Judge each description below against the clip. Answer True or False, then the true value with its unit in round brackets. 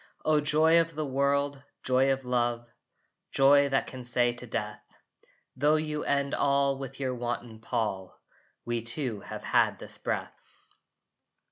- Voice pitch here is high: False (135 Hz)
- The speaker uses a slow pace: False (145 wpm)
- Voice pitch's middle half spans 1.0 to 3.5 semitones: True (2.8 semitones)